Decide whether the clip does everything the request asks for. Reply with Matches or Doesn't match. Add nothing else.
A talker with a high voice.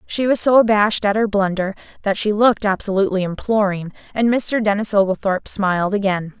Matches